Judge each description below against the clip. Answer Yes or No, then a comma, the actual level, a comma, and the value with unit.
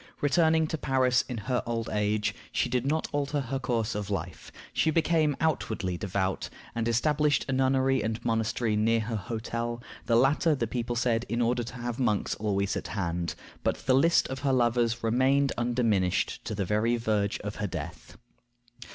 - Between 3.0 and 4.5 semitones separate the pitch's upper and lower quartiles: Yes, average, 3.6 semitones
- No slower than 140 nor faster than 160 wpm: No, average, 175 wpm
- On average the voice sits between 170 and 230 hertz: No, low, 120 Hz